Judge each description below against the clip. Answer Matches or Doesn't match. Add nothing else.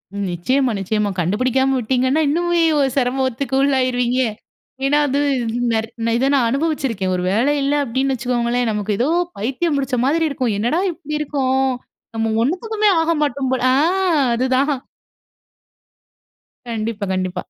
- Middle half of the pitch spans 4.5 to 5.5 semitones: Doesn't match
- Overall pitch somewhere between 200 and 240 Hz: Doesn't match